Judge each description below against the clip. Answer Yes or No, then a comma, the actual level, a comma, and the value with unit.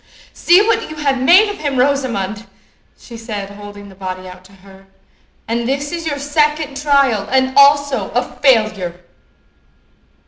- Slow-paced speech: No, average, 150 wpm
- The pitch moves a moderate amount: No, wide, 6.1 semitones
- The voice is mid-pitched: No, very high, 260 Hz